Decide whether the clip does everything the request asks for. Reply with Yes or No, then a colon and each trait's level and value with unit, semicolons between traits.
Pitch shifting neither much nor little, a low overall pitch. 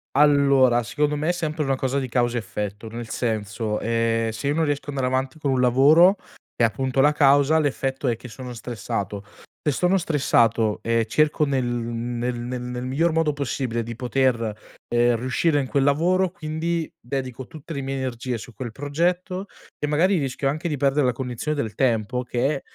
Yes: average, 3.8 semitones; low, 130 Hz